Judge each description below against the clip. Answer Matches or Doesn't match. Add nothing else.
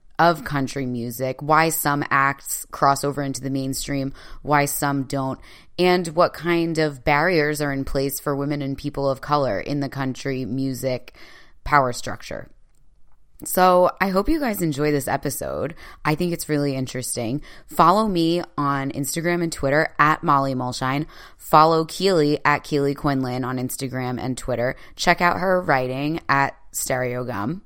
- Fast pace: Doesn't match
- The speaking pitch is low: Doesn't match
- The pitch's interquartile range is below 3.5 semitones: Matches